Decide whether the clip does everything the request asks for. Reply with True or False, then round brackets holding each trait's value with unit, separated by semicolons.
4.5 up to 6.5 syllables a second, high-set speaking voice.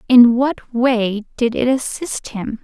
False (3.5 syllables/s; 240 Hz)